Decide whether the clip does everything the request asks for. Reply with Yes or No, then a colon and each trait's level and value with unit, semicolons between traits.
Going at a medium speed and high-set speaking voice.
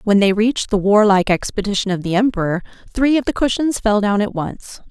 No: fast, 210 wpm; high, 210 Hz